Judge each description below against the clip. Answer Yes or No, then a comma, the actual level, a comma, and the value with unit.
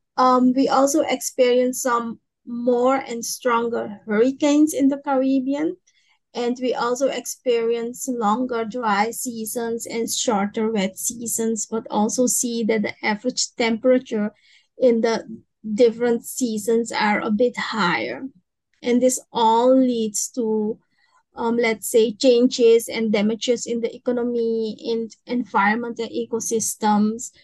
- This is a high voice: Yes, high, 235 Hz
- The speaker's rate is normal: No, slow, 120 wpm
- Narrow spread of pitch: Yes, narrow, 2.0 semitones